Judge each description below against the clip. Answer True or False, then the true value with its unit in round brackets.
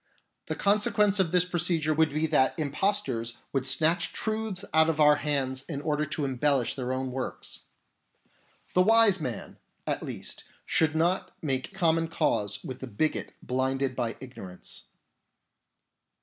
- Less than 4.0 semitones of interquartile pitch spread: False (4.8 semitones)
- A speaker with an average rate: True (145 wpm)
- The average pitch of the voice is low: False (150 Hz)